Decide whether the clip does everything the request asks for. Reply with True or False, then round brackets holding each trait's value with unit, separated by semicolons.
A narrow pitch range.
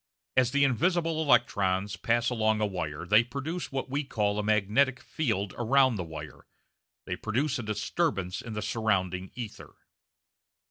False (4.8 semitones)